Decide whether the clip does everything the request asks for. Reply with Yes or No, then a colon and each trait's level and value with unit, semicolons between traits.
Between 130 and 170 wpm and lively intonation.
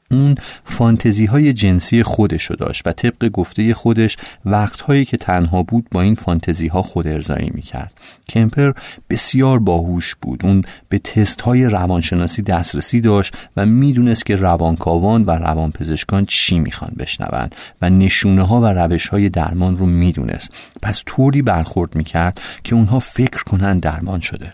No: average, 150 wpm; average, 5.0 semitones